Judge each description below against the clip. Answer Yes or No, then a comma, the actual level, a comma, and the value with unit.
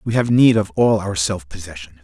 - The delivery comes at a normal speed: No, fast, 235 wpm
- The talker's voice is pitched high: No, very low, 95 Hz